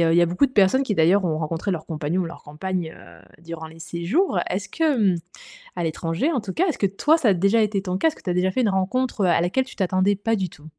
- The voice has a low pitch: No, high, 190 Hz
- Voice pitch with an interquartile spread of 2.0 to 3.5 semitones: No, average, 4.8 semitones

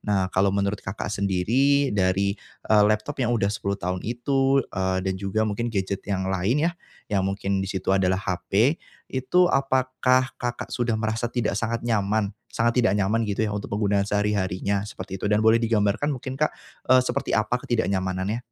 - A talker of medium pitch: No, low, 105 Hz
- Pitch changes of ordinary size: Yes, average, 3.6 semitones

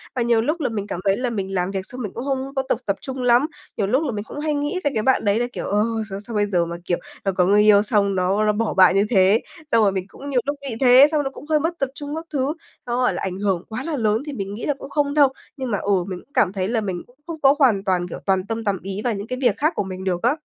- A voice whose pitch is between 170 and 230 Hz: Yes, high, 225 Hz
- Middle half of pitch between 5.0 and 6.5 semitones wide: Yes, wide, 5.5 semitones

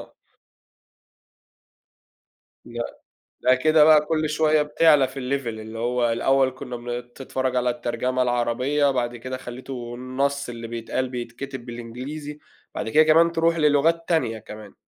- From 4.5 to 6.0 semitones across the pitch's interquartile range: No, average, 3.7 semitones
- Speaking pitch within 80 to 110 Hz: No, low, 130 Hz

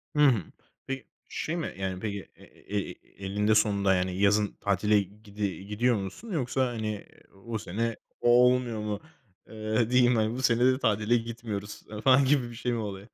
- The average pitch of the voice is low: Yes, low, 110 Hz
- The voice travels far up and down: No, average, 3.2 semitones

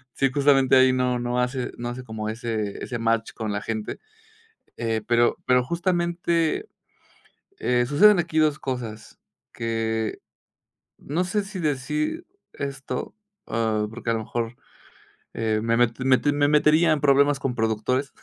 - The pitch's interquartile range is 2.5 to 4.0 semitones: No, average, 4.4 semitones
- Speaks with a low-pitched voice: Yes, low, 125 Hz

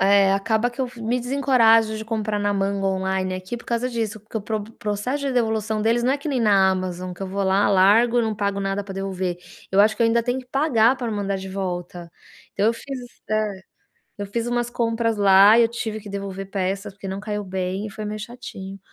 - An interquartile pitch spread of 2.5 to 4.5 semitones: Yes, average, 3.0 semitones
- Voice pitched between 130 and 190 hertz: No, high, 210 Hz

